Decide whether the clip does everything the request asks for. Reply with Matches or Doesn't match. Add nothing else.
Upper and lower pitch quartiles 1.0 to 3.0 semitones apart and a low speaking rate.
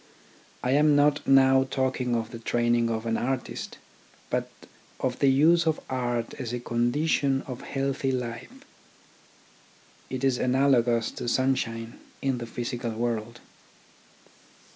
Matches